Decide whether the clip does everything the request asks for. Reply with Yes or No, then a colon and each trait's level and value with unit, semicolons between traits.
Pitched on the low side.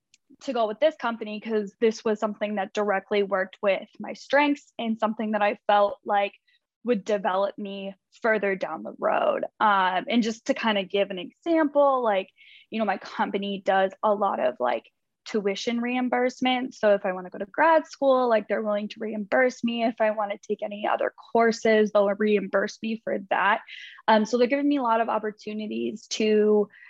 No: high, 215 Hz